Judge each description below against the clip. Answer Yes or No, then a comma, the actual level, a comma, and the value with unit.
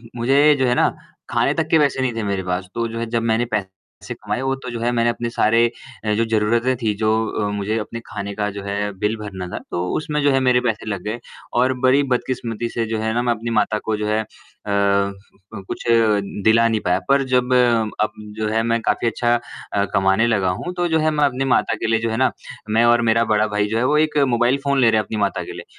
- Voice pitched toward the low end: Yes, low, 115 Hz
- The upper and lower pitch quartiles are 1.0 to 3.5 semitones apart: Yes, average, 2.8 semitones